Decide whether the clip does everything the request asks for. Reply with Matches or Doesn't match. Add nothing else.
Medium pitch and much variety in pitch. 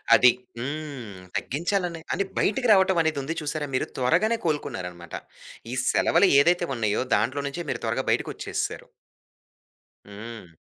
Matches